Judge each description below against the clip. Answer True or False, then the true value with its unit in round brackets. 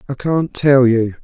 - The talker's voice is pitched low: True (130 Hz)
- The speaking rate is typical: True (195 wpm)